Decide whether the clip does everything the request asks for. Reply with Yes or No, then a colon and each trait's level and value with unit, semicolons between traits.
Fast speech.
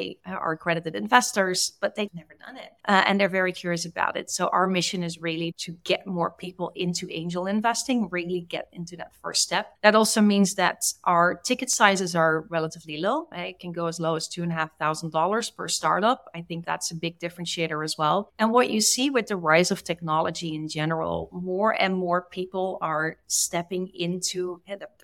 No: average, 190 wpm